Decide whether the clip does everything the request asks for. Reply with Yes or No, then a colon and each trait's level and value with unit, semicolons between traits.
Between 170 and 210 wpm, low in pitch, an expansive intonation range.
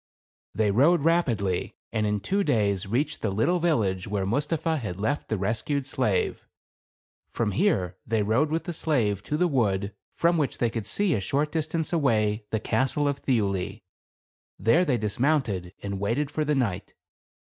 Yes: average, 180 wpm; low, 115 Hz; wide, 6.7 semitones